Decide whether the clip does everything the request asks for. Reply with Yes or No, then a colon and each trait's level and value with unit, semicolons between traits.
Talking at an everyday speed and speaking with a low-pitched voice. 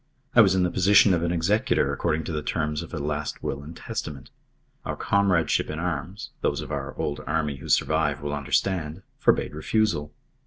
Yes: average, 190 wpm; very low, 80 Hz